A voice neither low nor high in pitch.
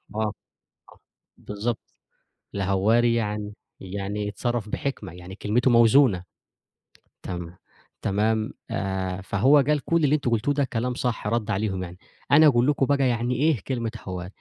No: low, 110 Hz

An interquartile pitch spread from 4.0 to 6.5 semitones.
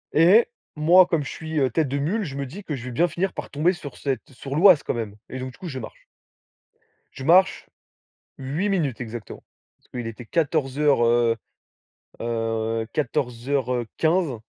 Yes: average, 5.3 semitones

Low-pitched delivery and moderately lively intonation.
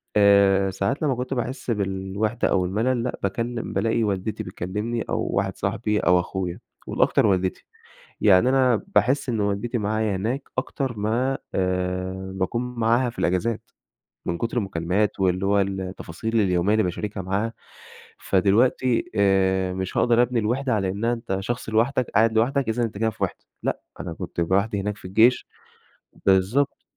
Yes: low, 105 Hz; average, 3.7 semitones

